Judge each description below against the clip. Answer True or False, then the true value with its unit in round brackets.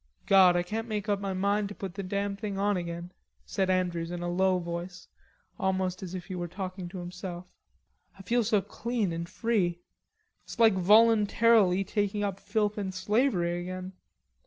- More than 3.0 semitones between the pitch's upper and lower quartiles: False (2.5 semitones)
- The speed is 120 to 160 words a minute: False (180 wpm)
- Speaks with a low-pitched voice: False (190 Hz)